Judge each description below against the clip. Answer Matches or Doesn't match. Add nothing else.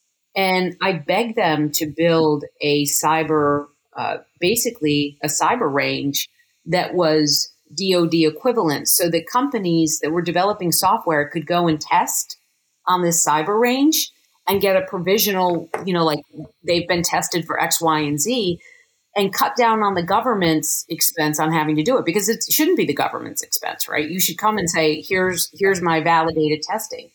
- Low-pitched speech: Doesn't match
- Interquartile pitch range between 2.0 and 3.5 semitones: Doesn't match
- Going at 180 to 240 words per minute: Doesn't match